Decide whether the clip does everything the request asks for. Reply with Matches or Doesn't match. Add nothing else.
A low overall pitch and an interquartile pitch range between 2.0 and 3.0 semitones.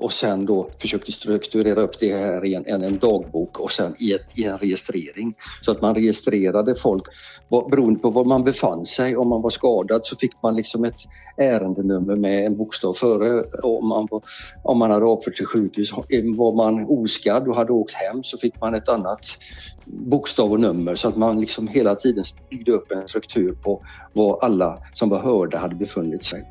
Matches